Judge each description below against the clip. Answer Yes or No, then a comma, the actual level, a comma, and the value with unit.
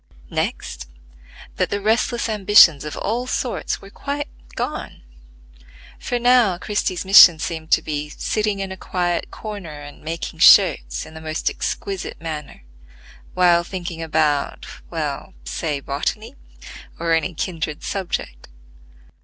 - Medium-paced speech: No, slow, 125 wpm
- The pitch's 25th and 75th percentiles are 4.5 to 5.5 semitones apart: Yes, average, 4.9 semitones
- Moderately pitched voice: Yes, medium, 175 Hz